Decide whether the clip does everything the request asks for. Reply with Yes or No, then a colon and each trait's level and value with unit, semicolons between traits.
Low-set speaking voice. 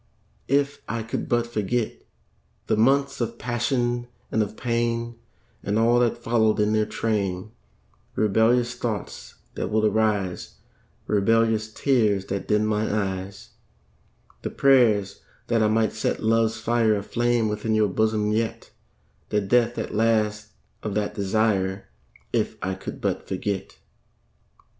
Yes: low, 110 Hz